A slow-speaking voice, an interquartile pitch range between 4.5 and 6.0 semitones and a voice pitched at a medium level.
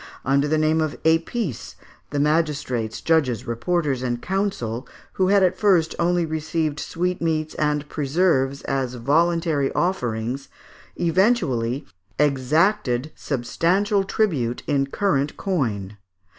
Yes: slow, 110 wpm; average, 4.8 semitones; medium, 150 Hz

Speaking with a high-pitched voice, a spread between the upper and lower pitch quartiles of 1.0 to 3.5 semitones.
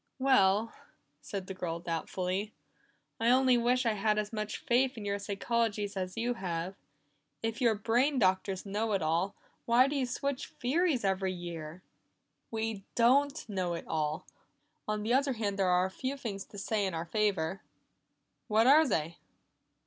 No: high, 210 Hz; average, 4.4 semitones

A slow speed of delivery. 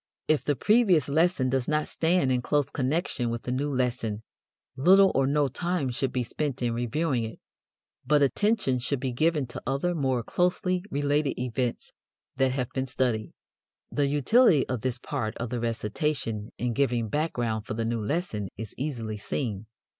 No: average, 170 wpm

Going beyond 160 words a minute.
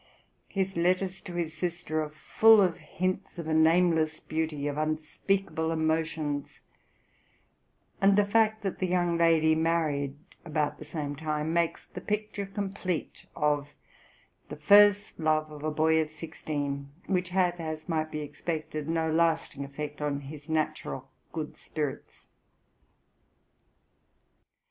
No: slow, 135 wpm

